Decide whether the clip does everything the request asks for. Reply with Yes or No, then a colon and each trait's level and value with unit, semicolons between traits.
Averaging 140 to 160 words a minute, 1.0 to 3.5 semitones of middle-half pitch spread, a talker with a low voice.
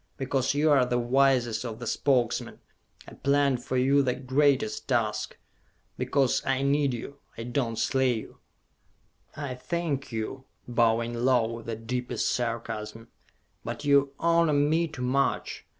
Yes: average, 150 wpm; average, 3.0 semitones; low, 130 Hz